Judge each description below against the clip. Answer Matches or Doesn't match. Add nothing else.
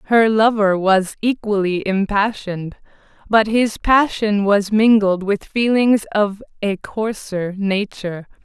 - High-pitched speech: Matches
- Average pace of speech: Doesn't match